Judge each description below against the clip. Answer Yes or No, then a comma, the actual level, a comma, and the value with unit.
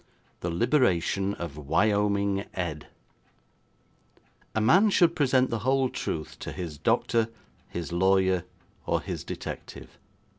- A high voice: No, low, 100 Hz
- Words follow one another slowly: Yes, slow, 115 wpm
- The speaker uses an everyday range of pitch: No, wide, 6.2 semitones